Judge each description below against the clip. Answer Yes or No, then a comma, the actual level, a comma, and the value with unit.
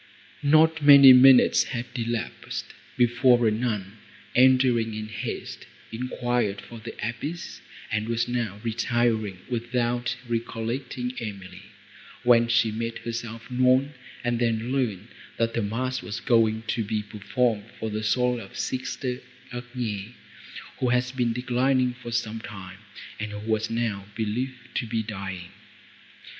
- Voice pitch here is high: No, low, 120 Hz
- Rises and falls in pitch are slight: Yes, narrow, 2.3 semitones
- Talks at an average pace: No, slow, 130 wpm